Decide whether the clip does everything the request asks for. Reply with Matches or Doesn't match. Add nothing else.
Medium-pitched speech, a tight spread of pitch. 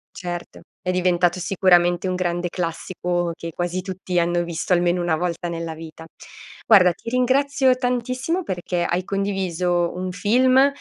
Matches